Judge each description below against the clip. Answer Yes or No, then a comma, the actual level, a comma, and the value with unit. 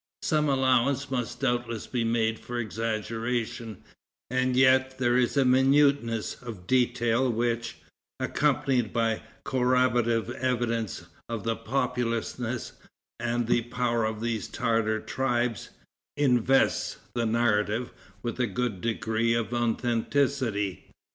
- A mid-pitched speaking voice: No, low, 120 Hz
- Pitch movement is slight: Yes, narrow, 2.0 semitones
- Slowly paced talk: Yes, slow, 115 wpm